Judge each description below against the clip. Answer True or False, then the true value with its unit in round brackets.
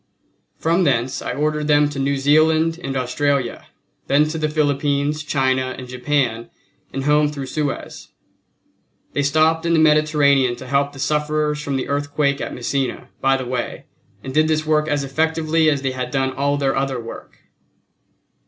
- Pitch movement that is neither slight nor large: False (2.3 semitones)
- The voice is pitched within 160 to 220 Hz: False (145 Hz)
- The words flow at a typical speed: True (170 wpm)